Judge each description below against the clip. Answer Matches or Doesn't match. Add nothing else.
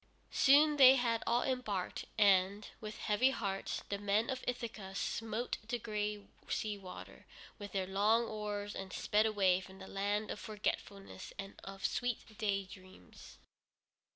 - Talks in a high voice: Matches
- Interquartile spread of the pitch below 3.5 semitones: Matches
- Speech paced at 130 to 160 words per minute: Matches